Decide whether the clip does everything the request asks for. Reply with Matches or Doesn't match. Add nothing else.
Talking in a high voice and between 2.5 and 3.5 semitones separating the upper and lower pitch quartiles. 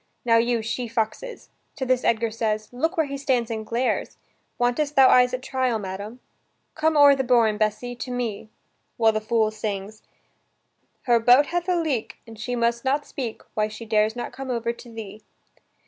Matches